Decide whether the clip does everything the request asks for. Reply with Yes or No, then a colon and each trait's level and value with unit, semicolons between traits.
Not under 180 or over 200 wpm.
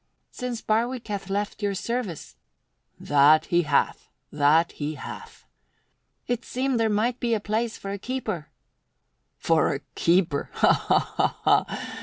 No: average, 145 wpm